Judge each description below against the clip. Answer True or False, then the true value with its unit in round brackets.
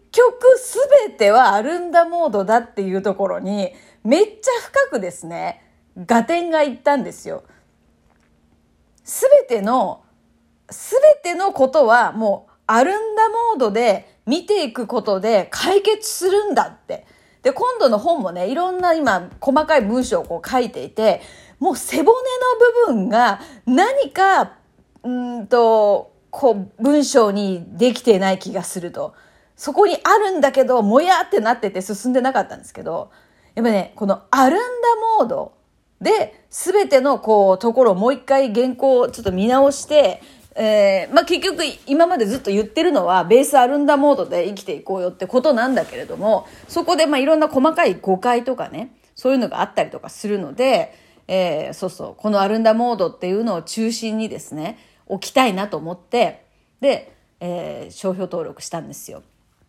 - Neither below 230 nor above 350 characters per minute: True (315 characters per minute)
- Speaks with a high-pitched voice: True (255 Hz)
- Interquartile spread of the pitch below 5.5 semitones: False (7.9 semitones)